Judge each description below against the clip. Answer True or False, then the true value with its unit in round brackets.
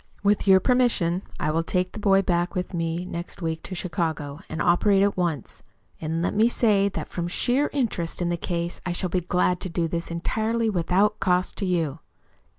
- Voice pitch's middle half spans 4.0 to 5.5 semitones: False (2.8 semitones)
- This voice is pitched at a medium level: True (180 Hz)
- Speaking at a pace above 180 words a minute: True (200 wpm)